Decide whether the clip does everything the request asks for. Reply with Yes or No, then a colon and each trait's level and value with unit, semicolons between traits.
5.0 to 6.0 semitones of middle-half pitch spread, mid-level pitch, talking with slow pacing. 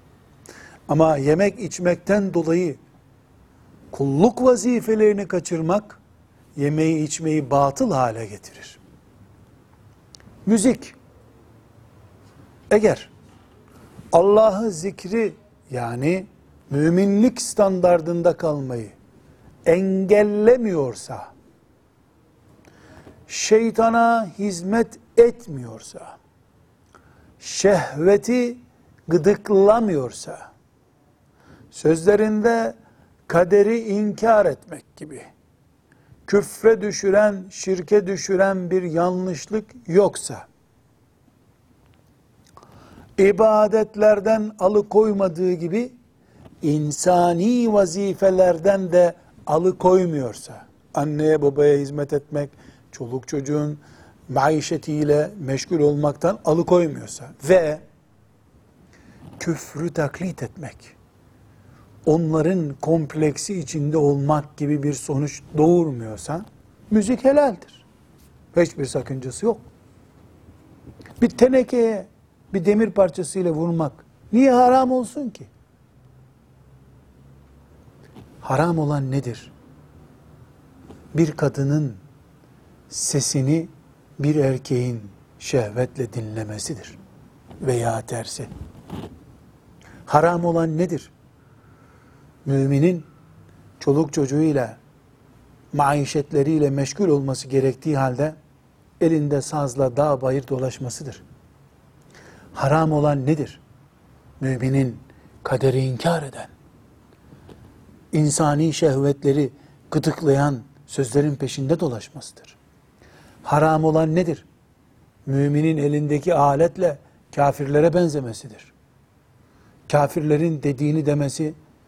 Yes: wide, 5.5 semitones; medium, 150 Hz; slow, 65 wpm